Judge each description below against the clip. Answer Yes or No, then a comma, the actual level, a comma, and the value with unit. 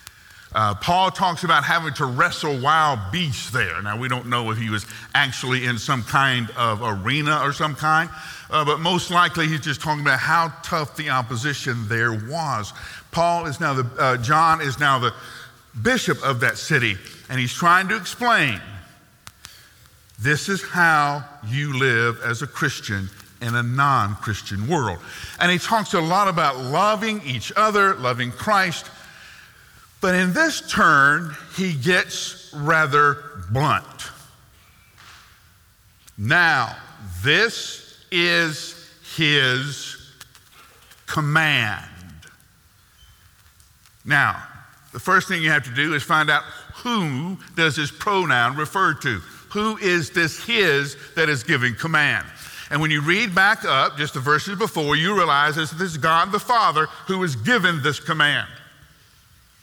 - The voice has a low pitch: No, medium, 145 Hz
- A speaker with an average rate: Yes, average, 145 wpm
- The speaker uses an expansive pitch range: Yes, wide, 5.9 semitones